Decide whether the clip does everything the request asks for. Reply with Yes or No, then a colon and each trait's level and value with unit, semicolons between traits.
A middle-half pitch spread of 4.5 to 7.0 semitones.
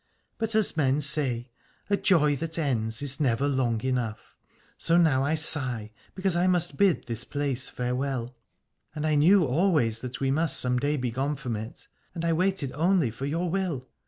Yes: average, 4.8 semitones